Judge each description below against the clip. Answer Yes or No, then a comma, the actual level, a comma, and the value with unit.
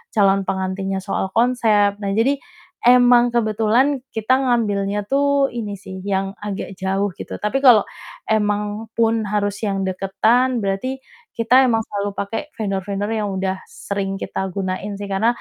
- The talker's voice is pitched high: Yes, high, 205 Hz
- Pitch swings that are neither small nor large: Yes, average, 3.1 semitones